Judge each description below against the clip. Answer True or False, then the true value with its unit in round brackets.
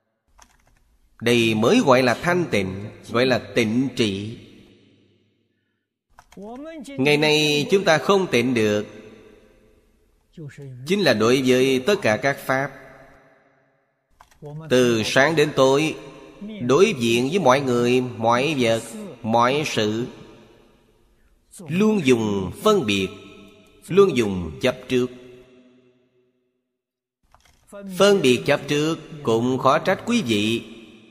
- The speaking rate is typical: False (105 wpm)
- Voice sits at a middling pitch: False (125 Hz)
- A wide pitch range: False (4.6 semitones)